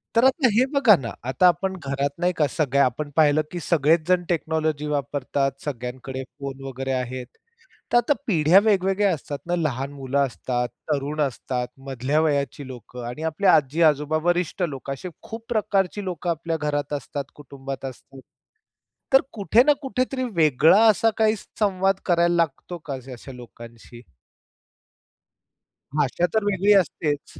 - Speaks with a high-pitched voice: No, medium, 150 Hz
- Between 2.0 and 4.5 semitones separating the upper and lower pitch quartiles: No, average, 5.3 semitones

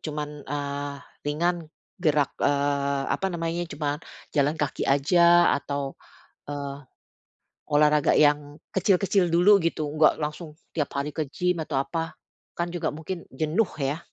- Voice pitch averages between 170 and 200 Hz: No, medium, 150 Hz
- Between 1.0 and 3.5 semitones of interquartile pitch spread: Yes, average, 3.0 semitones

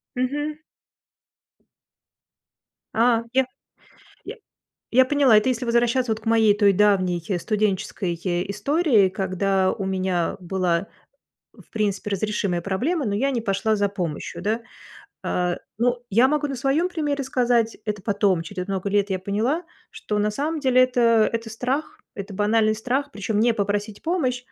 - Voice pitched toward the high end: Yes, high, 220 Hz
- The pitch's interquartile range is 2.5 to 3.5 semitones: No, average, 4.3 semitones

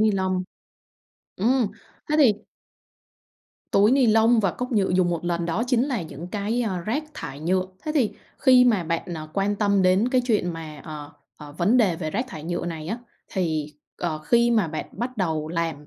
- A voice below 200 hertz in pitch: Yes, high, 190 Hz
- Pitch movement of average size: No, wide, 5.8 semitones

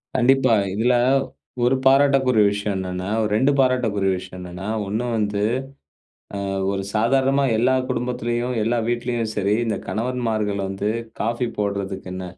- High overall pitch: No, low, 115 Hz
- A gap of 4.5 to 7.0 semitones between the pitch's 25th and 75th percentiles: No, average, 3.7 semitones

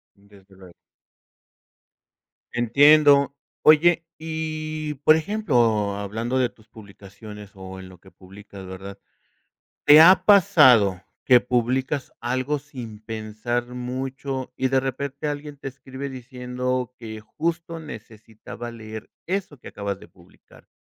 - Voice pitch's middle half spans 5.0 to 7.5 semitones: Yes, average, 5.3 semitones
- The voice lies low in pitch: Yes, low, 125 Hz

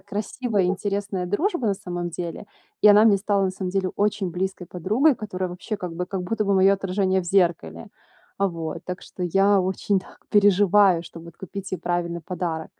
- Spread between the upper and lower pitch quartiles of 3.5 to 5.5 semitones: No, narrow, 2.4 semitones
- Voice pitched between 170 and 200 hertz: Yes, high, 190 Hz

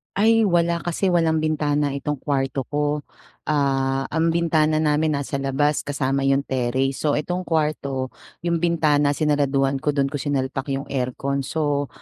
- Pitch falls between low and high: Yes, medium, 145 Hz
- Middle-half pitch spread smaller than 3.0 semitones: Yes, narrow, 2.4 semitones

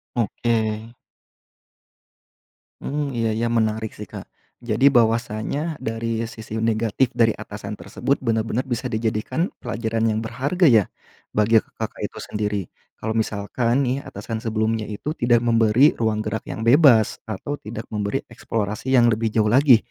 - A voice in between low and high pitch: No, low, 115 Hz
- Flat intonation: Yes, narrow, 1.7 semitones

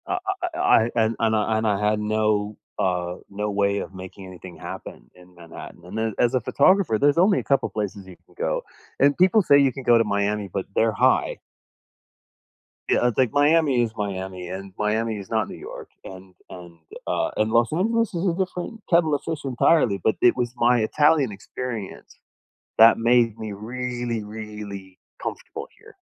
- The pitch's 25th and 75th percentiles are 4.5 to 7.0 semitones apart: Yes, average, 5.0 semitones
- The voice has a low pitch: Yes, low, 110 Hz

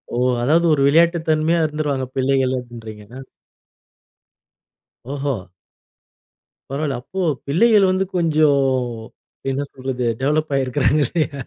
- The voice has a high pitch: No, medium, 145 Hz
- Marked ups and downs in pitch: No, average, 3.3 semitones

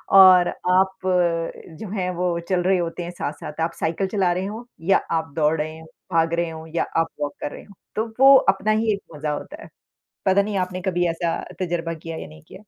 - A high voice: No, medium, 175 Hz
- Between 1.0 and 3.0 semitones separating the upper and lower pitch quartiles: Yes, narrow, 2.6 semitones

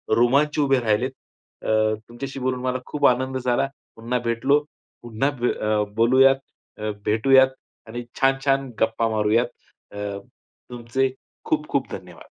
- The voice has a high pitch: No, low, 125 Hz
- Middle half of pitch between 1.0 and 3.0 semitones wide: Yes, average, 2.7 semitones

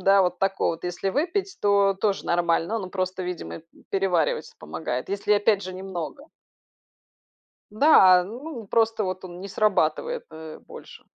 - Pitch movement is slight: No, average, 3.1 semitones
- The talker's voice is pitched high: Yes, high, 195 Hz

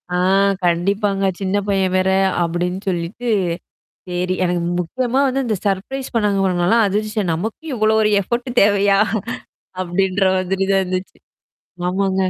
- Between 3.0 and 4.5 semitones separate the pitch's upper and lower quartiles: No, narrow, 2.6 semitones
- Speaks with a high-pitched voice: Yes, high, 195 Hz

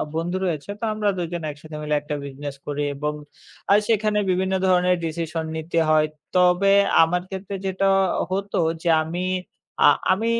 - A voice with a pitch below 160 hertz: No, medium, 175 Hz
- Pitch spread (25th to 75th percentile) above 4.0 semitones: No, average, 3.5 semitones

